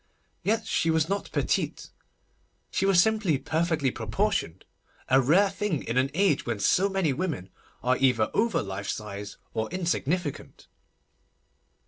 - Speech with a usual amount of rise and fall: No, wide, 8.3 semitones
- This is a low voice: No, medium, 155 Hz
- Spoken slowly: Yes, slow, 130 wpm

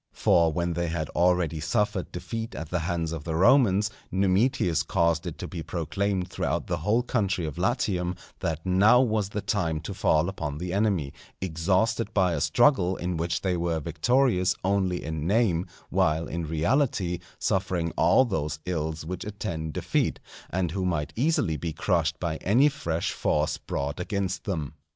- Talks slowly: No, average, 170 wpm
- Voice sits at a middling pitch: No, very low, 90 Hz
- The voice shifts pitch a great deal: No, average, 3.6 semitones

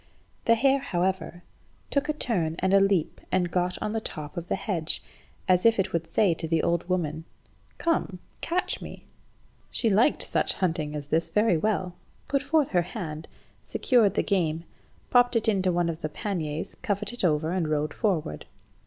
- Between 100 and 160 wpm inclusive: No, average, 180 wpm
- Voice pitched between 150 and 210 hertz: Yes, medium, 185 Hz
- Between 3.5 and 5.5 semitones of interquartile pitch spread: Yes, average, 5.0 semitones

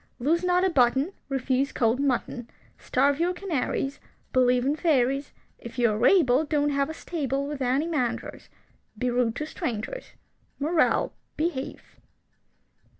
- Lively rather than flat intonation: No, average, 3.8 semitones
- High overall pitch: Yes, very high, 275 Hz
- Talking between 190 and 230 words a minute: No, average, 140 wpm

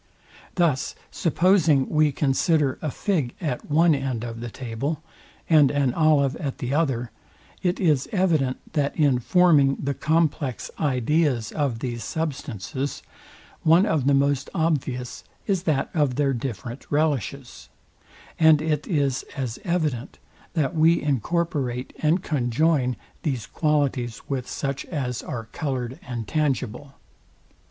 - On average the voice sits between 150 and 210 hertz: No, medium, 140 Hz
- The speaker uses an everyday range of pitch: Yes, average, 3.8 semitones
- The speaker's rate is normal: No, slow, 130 wpm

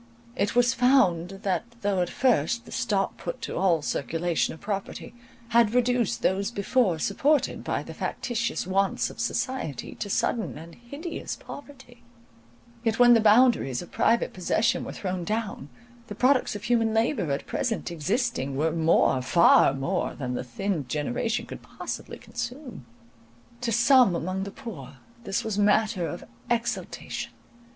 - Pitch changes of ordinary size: No, wide, 5.9 semitones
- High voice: Yes, high, 205 Hz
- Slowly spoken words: No, average, 150 wpm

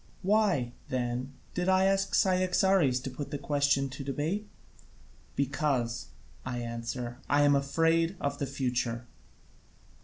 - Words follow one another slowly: Yes, slow, 125 wpm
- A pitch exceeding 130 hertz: Yes, medium, 140 Hz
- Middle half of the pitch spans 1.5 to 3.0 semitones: No, average, 4.9 semitones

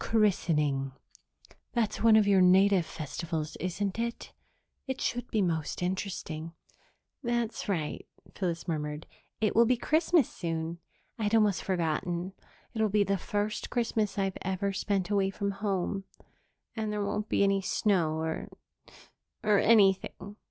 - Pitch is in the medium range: No, high, 195 Hz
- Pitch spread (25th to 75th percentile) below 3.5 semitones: No, average, 3.8 semitones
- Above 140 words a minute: No, slow, 135 wpm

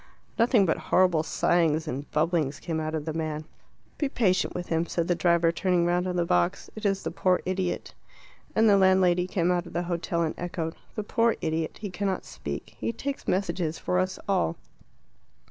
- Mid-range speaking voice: Yes, medium, 175 Hz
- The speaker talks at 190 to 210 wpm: Yes, average, 195 wpm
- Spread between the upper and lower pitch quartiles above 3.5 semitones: No, narrow, 2.5 semitones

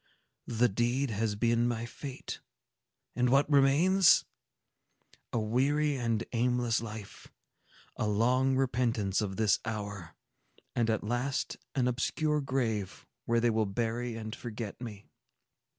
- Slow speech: Yes, slow, 120 wpm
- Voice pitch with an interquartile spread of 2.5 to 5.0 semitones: Yes, average, 2.8 semitones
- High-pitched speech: No, low, 120 Hz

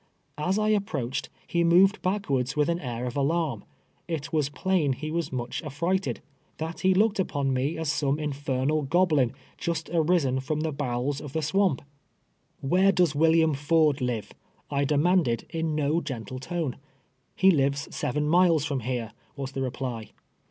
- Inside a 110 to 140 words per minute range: No, average, 170 wpm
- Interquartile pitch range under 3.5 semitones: No, average, 4.1 semitones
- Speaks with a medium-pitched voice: Yes, medium, 150 Hz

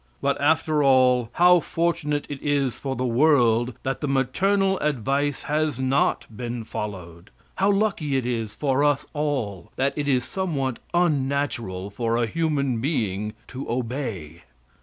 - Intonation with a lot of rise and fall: No, average, 4.0 semitones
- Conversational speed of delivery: Yes, average, 145 wpm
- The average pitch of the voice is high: No, low, 135 Hz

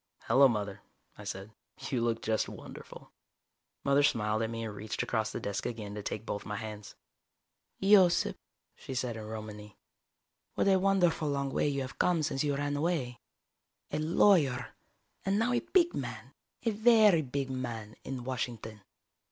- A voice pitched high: No, low, 130 Hz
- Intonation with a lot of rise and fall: Yes, wide, 6.5 semitones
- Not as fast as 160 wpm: No, average, 165 wpm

